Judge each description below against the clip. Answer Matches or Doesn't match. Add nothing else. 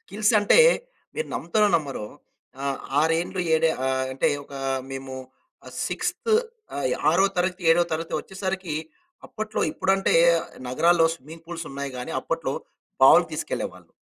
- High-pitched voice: Doesn't match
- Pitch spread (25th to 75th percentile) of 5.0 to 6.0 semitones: Matches